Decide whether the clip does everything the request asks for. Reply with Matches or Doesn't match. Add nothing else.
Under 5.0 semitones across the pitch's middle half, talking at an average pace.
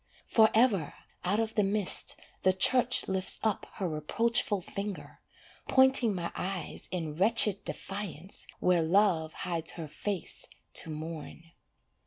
Doesn't match